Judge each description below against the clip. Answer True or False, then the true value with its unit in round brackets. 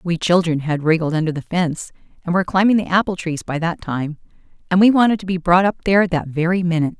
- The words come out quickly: True (230 wpm)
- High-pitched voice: False (175 Hz)